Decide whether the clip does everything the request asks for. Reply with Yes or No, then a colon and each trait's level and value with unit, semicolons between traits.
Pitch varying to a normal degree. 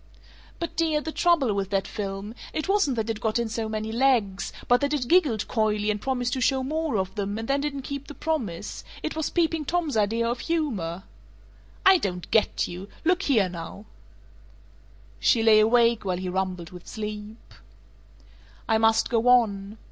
No: wide, 5.8 semitones